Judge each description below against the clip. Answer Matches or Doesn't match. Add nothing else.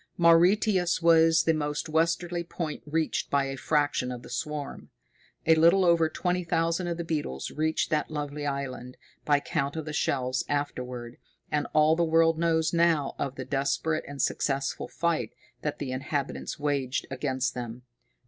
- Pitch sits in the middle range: Matches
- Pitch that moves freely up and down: Doesn't match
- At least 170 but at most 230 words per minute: Doesn't match